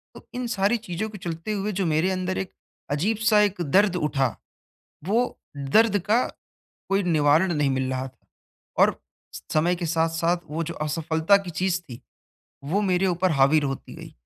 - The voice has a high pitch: No, medium, 175 Hz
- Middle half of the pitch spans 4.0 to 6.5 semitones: Yes, average, 4.7 semitones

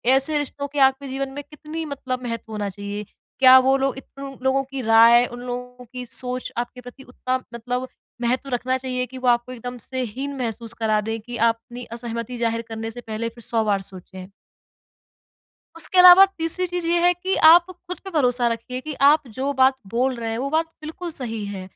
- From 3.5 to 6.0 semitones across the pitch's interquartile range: No, average, 3.0 semitones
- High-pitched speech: Yes, very high, 250 Hz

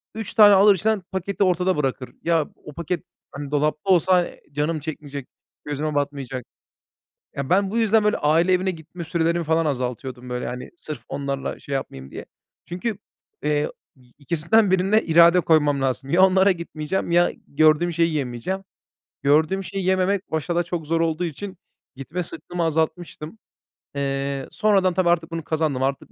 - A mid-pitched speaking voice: Yes, medium, 165 Hz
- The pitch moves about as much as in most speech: Yes, average, 4.3 semitones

